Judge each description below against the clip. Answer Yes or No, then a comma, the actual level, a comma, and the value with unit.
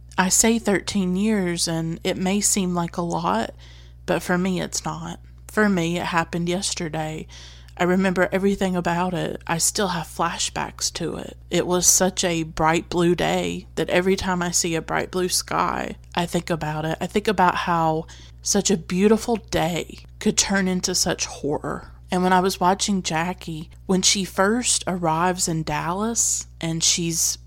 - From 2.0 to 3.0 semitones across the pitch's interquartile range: Yes, narrow, 2.6 semitones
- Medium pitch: Yes, medium, 175 Hz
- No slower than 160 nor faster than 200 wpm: Yes, average, 175 wpm